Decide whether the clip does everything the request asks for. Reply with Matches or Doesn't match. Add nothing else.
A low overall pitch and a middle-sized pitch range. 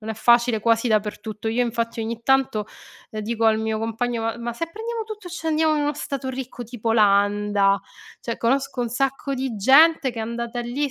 Doesn't match